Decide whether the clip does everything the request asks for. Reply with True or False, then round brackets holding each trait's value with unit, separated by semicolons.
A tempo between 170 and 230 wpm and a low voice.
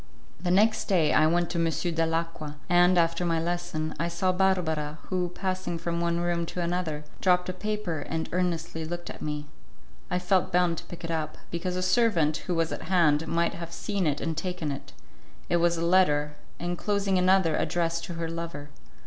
False (190 wpm; 170 Hz)